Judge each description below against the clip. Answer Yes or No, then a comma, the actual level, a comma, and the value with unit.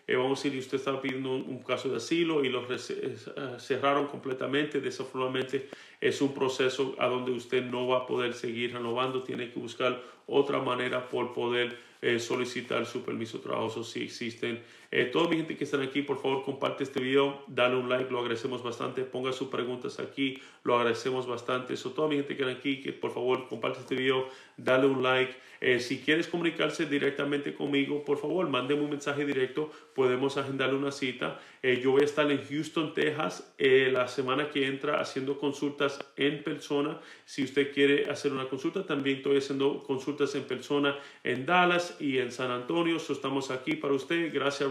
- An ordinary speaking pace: No, fast, 195 wpm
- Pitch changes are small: Yes, narrow, 1.8 semitones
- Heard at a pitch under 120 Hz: No, low, 135 Hz